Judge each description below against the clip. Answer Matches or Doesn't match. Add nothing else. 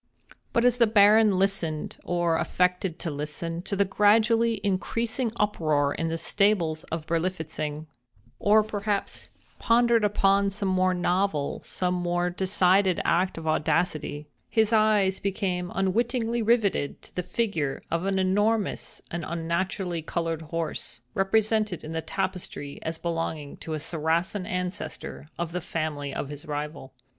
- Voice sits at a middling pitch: Matches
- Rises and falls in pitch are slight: Doesn't match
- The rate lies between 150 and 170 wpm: Doesn't match